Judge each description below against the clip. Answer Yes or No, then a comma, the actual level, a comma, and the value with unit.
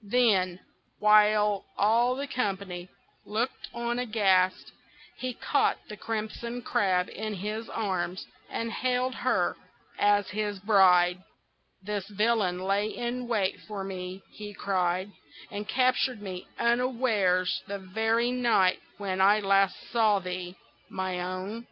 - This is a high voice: Yes, high, 205 Hz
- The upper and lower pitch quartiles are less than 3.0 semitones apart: No, average, 3.6 semitones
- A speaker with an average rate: No, slow, 125 wpm